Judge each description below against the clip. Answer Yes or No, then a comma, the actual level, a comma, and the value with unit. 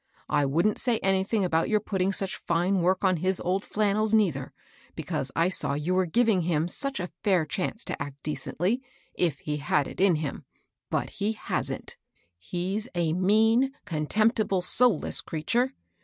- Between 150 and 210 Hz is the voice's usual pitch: Yes, medium, 185 Hz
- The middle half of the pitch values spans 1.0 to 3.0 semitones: No, average, 4.6 semitones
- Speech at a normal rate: Yes, average, 165 wpm